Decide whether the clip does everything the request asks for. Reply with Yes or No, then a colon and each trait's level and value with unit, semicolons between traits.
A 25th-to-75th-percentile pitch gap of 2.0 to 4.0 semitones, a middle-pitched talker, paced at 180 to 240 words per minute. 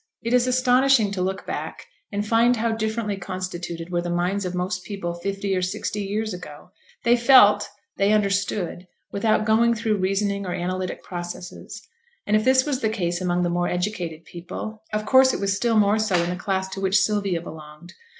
No: average, 3.4 semitones; high, 200 Hz; average, 190 wpm